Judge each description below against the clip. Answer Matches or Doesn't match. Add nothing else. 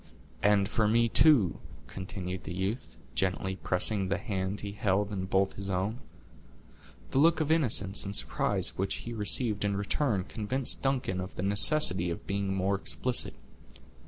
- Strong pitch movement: Doesn't match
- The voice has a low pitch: Matches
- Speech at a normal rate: Matches